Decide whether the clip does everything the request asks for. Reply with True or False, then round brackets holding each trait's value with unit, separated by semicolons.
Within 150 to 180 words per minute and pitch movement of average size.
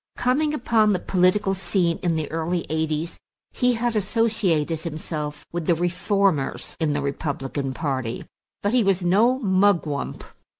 False (140 wpm; 5.0 semitones)